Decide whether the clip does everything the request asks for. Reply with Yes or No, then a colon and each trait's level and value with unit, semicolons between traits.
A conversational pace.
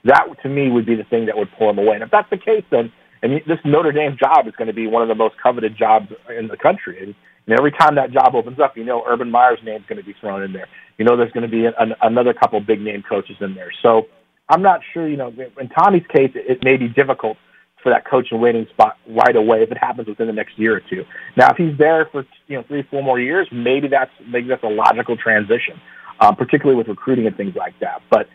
No: fast, 275 wpm